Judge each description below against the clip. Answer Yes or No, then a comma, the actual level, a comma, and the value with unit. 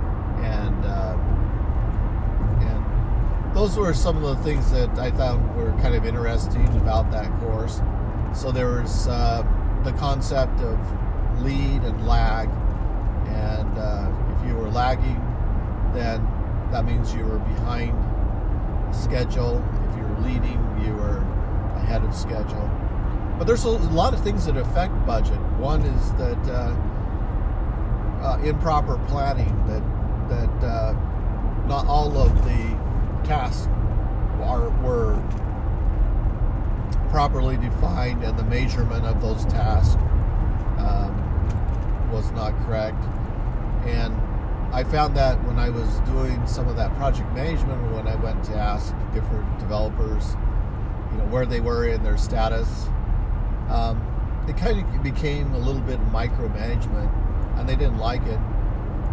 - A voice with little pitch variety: Yes, narrow, 1.9 semitones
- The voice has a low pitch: Yes, low, 110 Hz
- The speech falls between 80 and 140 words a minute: Yes, slow, 135 wpm